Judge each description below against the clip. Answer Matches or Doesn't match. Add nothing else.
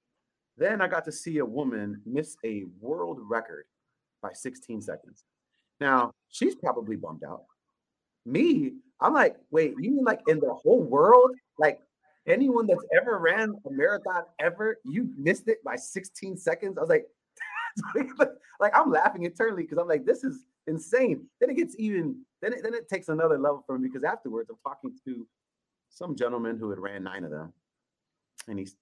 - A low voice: Doesn't match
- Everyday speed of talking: Matches